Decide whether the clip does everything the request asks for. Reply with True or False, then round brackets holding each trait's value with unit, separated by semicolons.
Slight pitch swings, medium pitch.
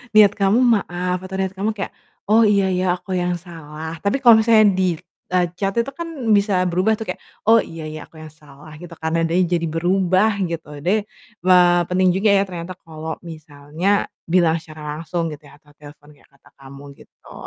False (3.7 semitones; 175 Hz)